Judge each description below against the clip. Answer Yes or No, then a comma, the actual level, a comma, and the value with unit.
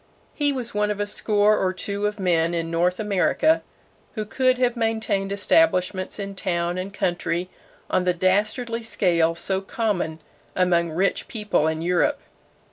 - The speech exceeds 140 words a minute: Yes, average, 155 wpm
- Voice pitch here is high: Yes, high, 195 Hz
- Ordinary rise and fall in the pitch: Yes, average, 3.2 semitones